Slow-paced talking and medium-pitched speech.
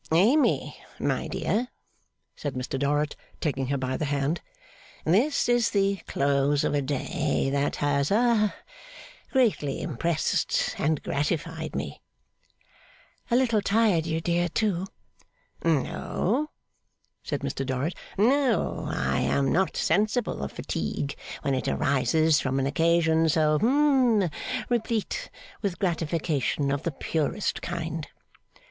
Yes: slow, 120 wpm; medium, 160 Hz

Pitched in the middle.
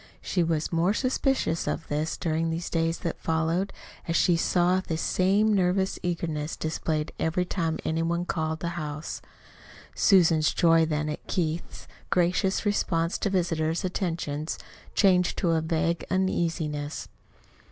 Yes: medium, 165 Hz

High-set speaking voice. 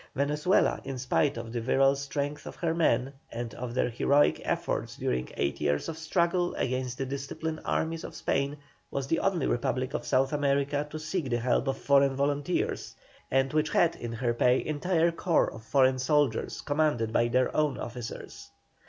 No: medium, 140 Hz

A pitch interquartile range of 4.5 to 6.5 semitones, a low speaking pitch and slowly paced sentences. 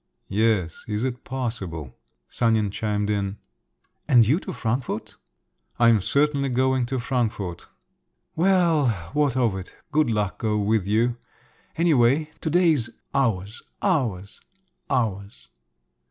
Yes: average, 4.8 semitones; low, 120 Hz; slow, 120 wpm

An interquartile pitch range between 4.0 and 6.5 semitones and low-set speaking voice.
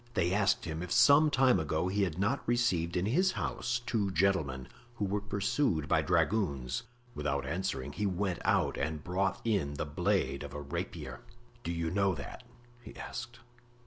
Yes: average, 5.0 semitones; very low, 95 Hz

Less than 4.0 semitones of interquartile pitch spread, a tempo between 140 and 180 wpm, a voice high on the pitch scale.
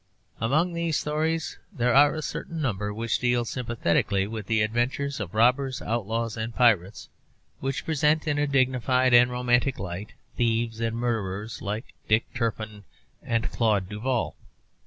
No: average, 3.4 semitones; average, 145 wpm; low, 120 Hz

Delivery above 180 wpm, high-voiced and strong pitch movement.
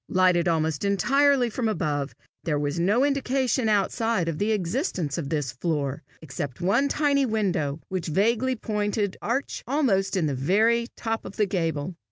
No: average, 160 wpm; high, 195 Hz; wide, 6.4 semitones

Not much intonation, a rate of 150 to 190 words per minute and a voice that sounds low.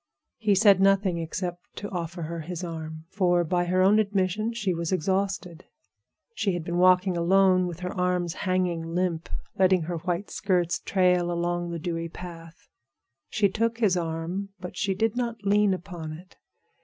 No: narrow, 2.2 semitones; average, 165 wpm; medium, 180 Hz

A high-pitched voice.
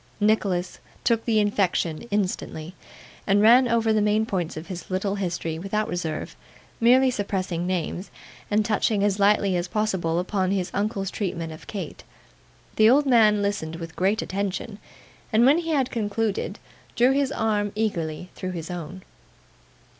Yes: high, 200 Hz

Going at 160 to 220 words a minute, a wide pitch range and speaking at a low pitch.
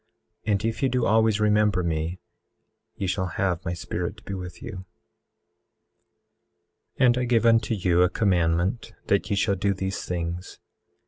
No: average, 165 wpm; average, 3.6 semitones; very low, 95 Hz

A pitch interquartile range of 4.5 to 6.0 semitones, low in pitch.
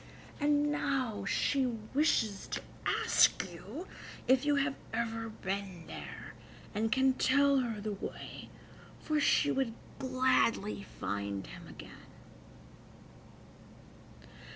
No: average, 4.8 semitones; high, 245 Hz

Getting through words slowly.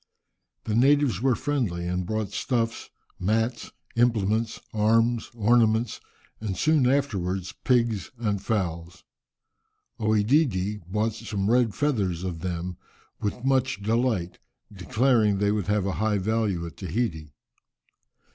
Yes: slow, 120 wpm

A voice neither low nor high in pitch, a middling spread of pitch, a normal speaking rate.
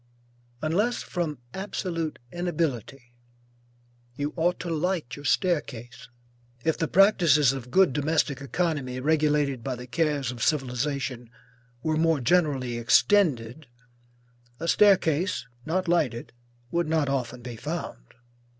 No: medium, 150 Hz; average, 4.9 semitones; slow, 115 wpm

